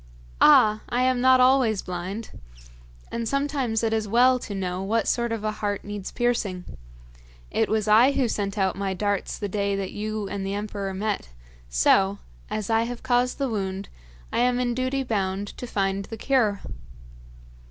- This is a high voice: Yes, high, 215 Hz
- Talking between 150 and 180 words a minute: Yes, average, 175 wpm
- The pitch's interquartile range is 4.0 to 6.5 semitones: No, average, 3.6 semitones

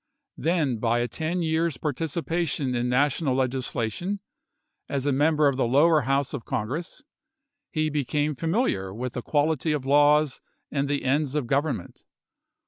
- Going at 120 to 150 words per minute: Yes, average, 145 wpm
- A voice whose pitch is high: No, medium, 145 Hz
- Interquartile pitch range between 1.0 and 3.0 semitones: No, average, 3.5 semitones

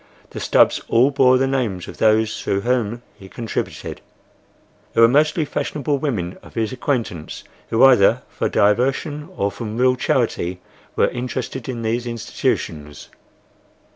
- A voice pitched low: Yes, low, 120 Hz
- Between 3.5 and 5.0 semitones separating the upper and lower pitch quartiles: Yes, average, 3.8 semitones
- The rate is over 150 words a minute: No, average, 140 wpm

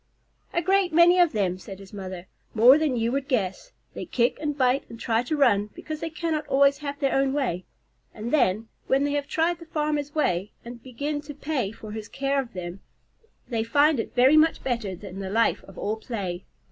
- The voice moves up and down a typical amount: No, wide, 6.0 semitones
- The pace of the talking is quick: Yes, fast, 210 wpm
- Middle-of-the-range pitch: No, very high, 260 Hz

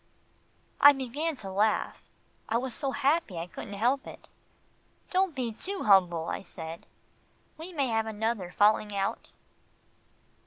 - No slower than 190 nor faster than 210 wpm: No, average, 140 wpm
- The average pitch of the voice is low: No, high, 225 Hz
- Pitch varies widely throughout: Yes, wide, 5.9 semitones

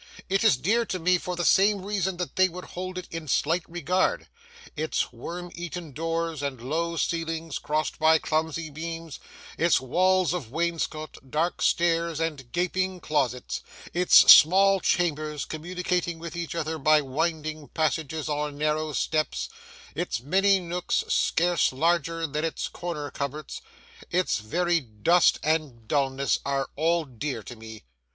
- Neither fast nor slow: Yes, average, 145 wpm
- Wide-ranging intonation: No, average, 2.8 semitones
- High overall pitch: No, medium, 165 Hz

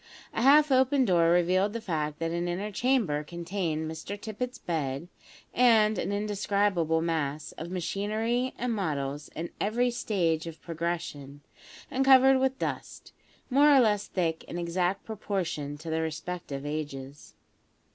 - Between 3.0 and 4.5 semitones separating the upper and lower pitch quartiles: No, wide, 5.5 semitones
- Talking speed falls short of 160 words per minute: Yes, average, 145 wpm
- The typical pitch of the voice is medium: Yes, medium, 180 Hz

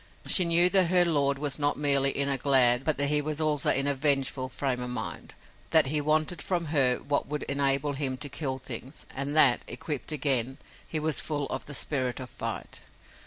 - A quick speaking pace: Yes, fast, 210 wpm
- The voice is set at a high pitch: No, medium, 140 Hz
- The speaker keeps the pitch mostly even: Yes, narrow, 2.3 semitones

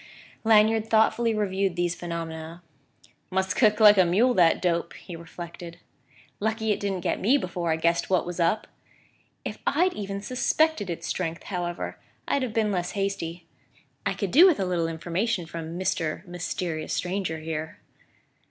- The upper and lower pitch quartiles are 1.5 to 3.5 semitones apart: No, average, 4.0 semitones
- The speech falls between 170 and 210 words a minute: No, average, 160 wpm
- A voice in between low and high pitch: Yes, medium, 180 Hz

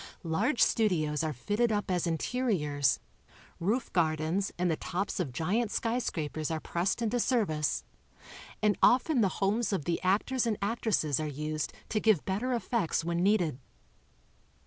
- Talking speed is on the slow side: No, average, 150 wpm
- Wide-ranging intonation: Yes, wide, 6.1 semitones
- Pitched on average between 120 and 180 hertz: No, high, 190 Hz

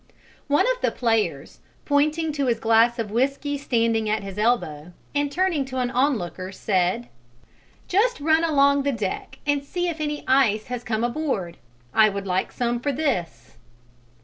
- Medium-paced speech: Yes, average, 165 wpm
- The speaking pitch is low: No, high, 245 Hz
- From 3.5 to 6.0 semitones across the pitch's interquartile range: Yes, average, 5.2 semitones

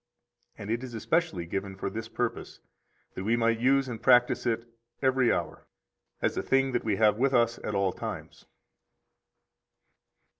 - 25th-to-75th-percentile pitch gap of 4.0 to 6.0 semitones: No, average, 3.3 semitones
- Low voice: Yes, low, 115 Hz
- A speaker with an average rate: Yes, average, 160 wpm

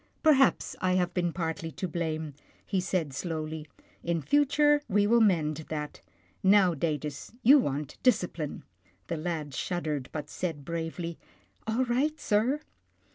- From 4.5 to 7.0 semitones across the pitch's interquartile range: Yes, average, 5.1 semitones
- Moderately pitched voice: Yes, medium, 170 Hz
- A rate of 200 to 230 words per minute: No, average, 150 wpm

